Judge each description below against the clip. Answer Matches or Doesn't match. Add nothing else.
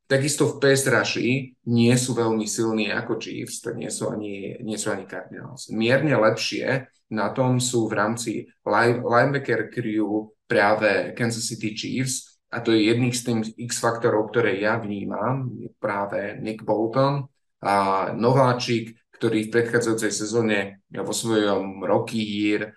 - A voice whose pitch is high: Doesn't match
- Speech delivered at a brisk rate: Doesn't match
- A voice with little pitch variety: Matches